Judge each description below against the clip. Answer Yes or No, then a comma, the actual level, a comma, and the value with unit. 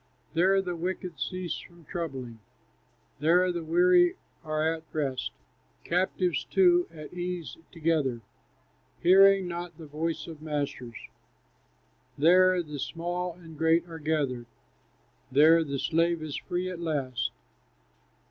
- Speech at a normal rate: No, slow, 120 wpm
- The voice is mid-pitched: Yes, medium, 165 Hz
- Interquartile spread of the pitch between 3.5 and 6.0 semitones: No, average, 2.7 semitones